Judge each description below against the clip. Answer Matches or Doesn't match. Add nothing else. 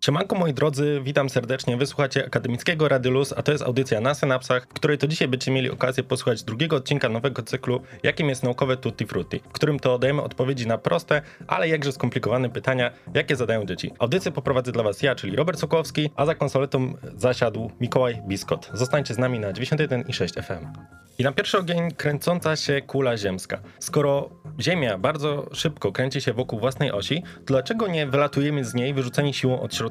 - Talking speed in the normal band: Doesn't match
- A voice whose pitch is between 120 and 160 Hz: Matches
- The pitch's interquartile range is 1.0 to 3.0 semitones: Matches